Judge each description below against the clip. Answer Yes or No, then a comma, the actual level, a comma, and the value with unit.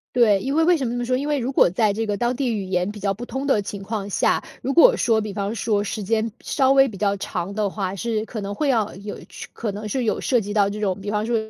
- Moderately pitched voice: No, high, 215 Hz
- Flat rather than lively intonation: No, average, 3.3 semitones